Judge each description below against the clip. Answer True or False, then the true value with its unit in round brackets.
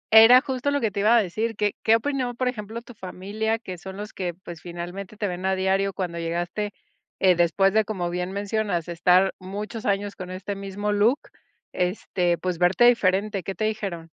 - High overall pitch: True (195 Hz)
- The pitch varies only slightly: False (3.2 semitones)